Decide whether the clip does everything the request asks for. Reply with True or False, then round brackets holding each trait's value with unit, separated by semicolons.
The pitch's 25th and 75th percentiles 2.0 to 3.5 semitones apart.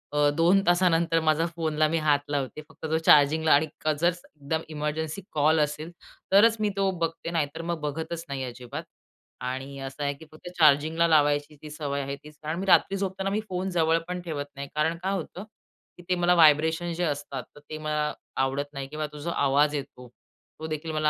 True (2.6 semitones)